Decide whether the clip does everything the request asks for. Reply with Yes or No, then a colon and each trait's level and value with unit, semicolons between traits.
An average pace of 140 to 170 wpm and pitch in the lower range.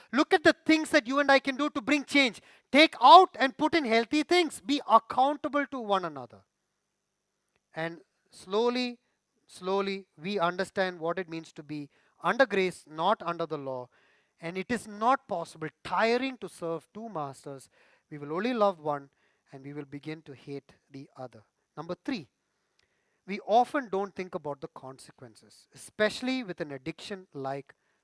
No: average, 165 wpm; high, 190 Hz